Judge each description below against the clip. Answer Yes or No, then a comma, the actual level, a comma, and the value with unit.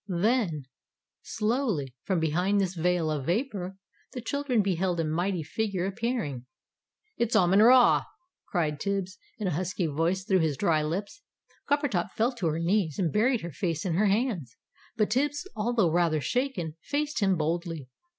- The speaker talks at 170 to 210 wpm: No, average, 160 wpm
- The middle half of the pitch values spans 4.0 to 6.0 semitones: Yes, average, 5.2 semitones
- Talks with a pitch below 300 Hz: Yes, medium, 185 Hz